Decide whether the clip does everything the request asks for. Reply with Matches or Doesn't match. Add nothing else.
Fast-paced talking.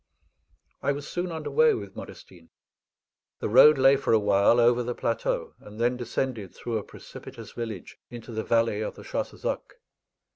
Doesn't match